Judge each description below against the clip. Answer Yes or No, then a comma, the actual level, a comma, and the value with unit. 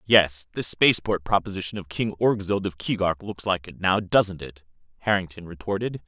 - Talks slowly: No, average, 170 wpm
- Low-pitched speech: Yes, very low, 95 Hz